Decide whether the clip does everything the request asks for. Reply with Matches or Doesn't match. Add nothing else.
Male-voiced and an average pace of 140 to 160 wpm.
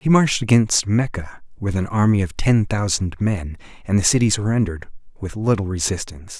Doesn't match